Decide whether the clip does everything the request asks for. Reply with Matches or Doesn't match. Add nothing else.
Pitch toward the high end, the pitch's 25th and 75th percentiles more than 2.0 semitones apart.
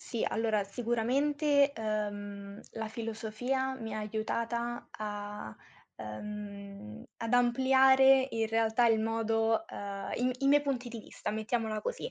Matches